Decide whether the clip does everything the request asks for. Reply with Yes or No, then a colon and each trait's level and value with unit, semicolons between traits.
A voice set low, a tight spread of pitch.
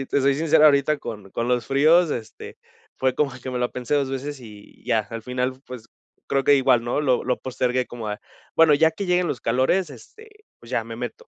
No: low, 130 Hz; average, 3.2 semitones